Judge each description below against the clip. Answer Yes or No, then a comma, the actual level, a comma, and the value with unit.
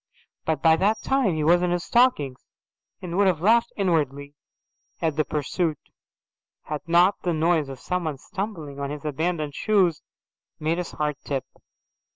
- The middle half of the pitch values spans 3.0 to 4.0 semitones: Yes, average, 3.5 semitones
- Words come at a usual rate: Yes, average, 160 wpm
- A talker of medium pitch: Yes, medium, 165 Hz